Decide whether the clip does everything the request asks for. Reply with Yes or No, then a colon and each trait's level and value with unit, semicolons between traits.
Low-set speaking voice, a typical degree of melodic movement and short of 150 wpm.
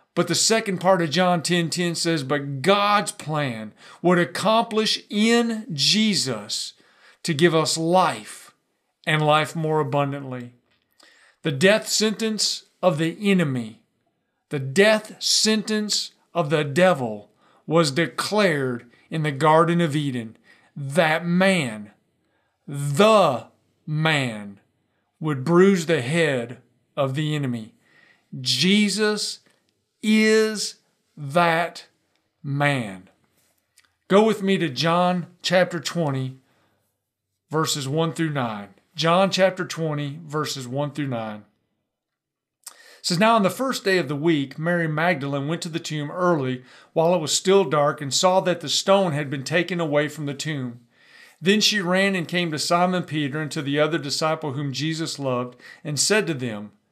No: medium, 160 Hz; average, 4.9 semitones; slow, 135 wpm